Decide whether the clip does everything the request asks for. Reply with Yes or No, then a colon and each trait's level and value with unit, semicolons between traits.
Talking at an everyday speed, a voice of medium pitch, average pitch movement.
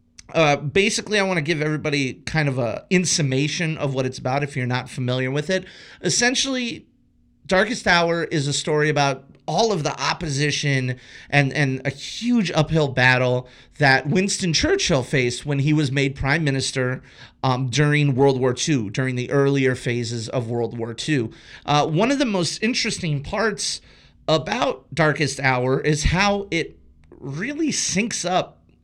Yes: average, 160 wpm; medium, 145 Hz; average, 4.9 semitones